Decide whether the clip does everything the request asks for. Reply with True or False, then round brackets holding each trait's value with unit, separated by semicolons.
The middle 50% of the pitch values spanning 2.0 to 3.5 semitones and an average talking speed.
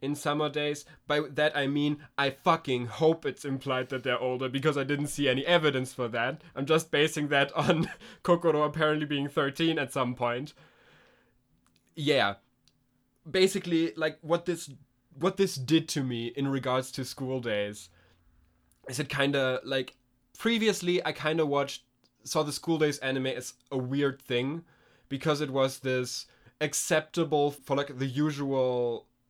True (3.1 semitones; 155 wpm)